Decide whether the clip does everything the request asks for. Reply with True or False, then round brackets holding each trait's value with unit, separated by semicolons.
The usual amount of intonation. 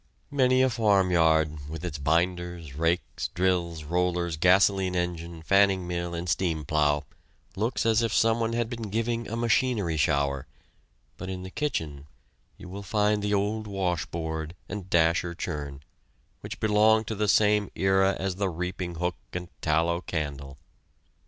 True (4.2 semitones)